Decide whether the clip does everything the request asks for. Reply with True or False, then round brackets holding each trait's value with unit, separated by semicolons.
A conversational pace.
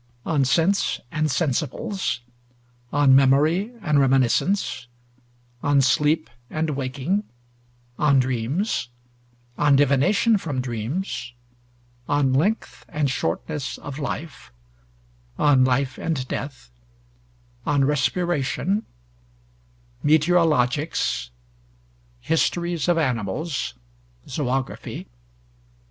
False (80 wpm)